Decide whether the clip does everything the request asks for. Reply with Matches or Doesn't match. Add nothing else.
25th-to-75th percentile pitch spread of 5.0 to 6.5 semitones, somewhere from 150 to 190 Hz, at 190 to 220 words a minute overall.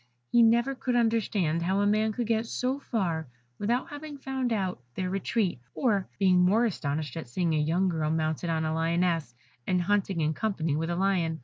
Matches